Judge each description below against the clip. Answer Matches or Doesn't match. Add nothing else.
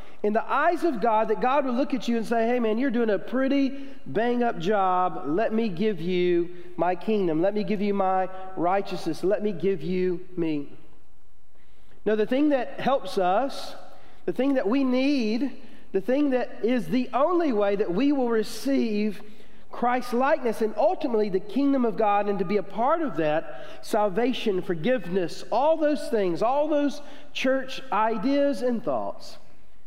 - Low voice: Doesn't match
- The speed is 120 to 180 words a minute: Matches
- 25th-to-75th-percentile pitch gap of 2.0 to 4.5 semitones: Doesn't match